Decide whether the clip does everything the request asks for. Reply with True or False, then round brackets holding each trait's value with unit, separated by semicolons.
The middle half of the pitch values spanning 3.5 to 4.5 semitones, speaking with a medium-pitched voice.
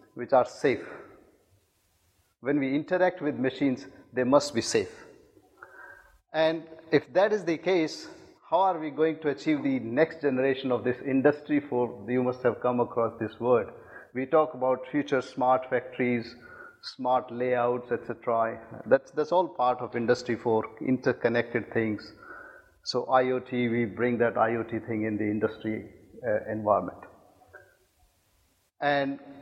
False (4.0 semitones; 125 Hz)